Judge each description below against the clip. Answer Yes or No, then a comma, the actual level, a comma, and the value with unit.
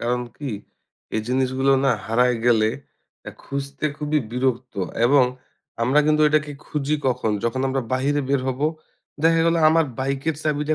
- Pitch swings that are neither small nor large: Yes, average, 3.0 semitones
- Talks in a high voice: No, low, 135 Hz